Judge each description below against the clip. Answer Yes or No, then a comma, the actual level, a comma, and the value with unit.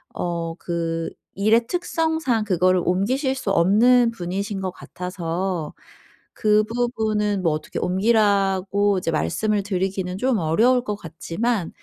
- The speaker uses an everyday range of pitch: Yes, average, 4.0 semitones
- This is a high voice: Yes, high, 200 Hz